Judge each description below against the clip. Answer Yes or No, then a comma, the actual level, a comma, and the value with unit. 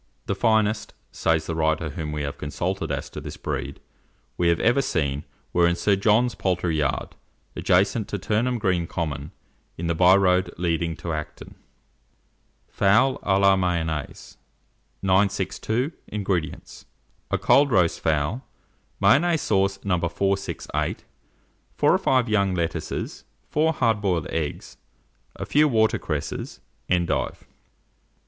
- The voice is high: No, very low, 95 Hz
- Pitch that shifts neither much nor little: Yes, average, 4.4 semitones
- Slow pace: Yes, slow, 130 wpm